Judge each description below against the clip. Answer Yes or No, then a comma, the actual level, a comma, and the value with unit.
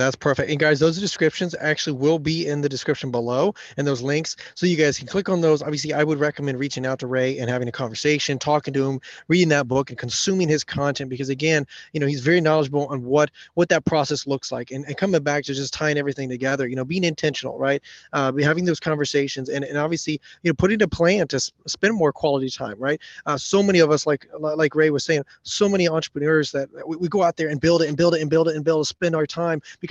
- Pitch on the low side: No, medium, 150 Hz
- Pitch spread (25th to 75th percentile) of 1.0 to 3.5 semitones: Yes, average, 2.8 semitones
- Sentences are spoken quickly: Yes, fast, 255 wpm